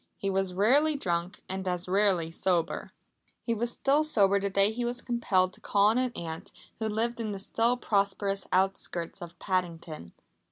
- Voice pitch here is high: Yes, high, 195 Hz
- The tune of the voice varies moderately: Yes, average, 3.6 semitones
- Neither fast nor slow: Yes, average, 170 wpm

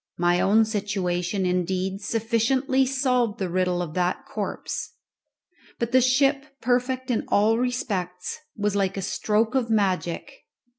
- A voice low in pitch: No, high, 215 Hz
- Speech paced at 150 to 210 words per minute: No, slow, 135 wpm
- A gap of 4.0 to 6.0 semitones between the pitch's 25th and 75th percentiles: Yes, wide, 5.4 semitones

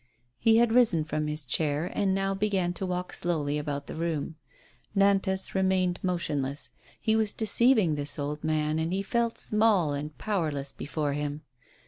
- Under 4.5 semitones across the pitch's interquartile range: No, average, 4.8 semitones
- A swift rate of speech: No, average, 160 wpm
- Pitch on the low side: No, medium, 170 Hz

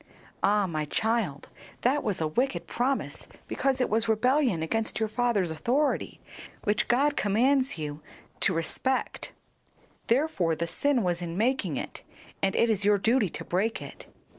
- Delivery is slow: No, average, 155 wpm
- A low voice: No, high, 220 Hz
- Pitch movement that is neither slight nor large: No, wide, 6.3 semitones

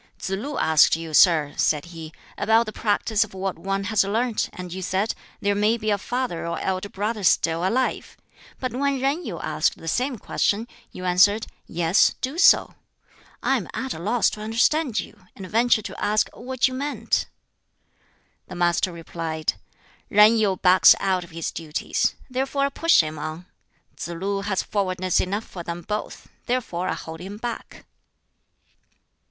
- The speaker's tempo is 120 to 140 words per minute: No, average, 170 wpm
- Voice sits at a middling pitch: No, high, 200 Hz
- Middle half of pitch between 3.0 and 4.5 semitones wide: No, average, 4.9 semitones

